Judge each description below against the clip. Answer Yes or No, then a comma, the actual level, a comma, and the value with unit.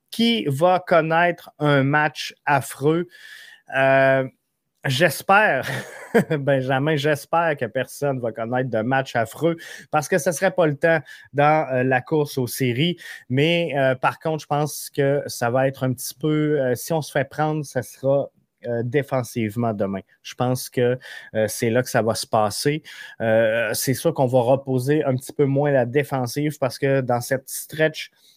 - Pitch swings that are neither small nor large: Yes, average, 3.4 semitones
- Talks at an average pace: Yes, average, 175 wpm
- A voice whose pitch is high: No, medium, 140 Hz